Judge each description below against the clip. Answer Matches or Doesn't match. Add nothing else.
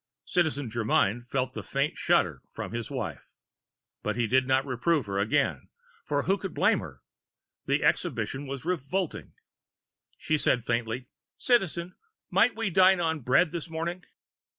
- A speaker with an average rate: Matches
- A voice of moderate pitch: Matches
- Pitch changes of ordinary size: Doesn't match